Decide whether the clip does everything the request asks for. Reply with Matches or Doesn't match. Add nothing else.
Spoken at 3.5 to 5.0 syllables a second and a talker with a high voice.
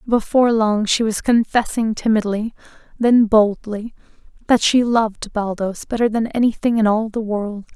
Matches